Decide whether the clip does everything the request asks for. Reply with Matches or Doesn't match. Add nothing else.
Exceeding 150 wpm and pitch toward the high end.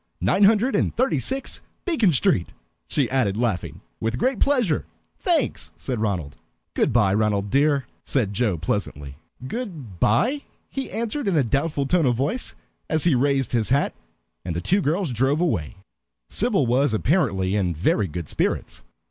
Doesn't match